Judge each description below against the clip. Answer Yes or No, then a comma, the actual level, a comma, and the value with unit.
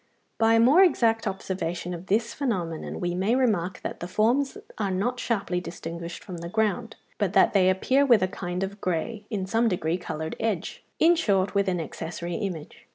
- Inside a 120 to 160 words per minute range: No, average, 190 wpm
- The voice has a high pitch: Yes, high, 195 Hz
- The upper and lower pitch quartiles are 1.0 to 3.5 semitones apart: No, average, 4.4 semitones